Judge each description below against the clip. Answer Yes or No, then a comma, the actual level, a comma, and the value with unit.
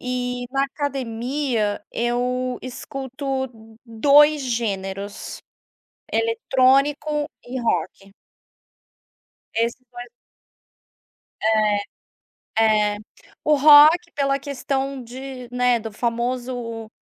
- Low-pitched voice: No, very high, 250 Hz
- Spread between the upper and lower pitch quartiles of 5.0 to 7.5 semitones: No, average, 3.0 semitones